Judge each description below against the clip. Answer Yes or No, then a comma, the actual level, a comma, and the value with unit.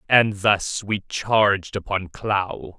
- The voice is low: Yes, low, 100 Hz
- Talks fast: No, slow, 130 wpm